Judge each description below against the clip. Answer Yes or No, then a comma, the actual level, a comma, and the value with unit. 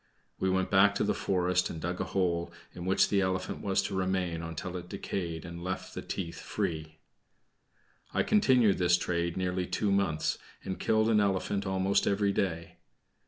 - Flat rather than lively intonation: Yes, narrow, 2.2 semitones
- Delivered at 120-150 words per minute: No, average, 175 wpm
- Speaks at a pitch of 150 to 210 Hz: No, very low, 95 Hz